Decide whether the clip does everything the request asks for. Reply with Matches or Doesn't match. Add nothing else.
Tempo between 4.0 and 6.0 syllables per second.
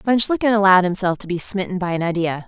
Doesn't match